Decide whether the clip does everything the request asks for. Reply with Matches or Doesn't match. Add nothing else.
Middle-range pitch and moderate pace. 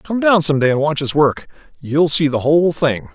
Doesn't match